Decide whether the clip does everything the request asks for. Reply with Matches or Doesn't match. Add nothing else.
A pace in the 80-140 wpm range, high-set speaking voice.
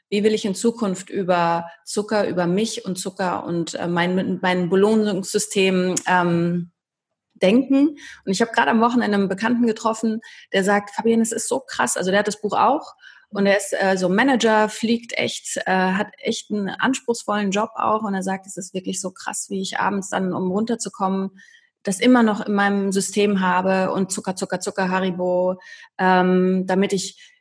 Doesn't match